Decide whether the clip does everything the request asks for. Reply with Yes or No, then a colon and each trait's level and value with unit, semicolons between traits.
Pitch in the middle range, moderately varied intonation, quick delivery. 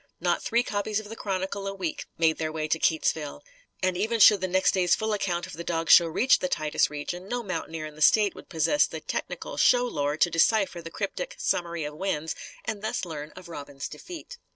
Yes: medium, 180 Hz; average, 4.5 semitones; fast, 220 wpm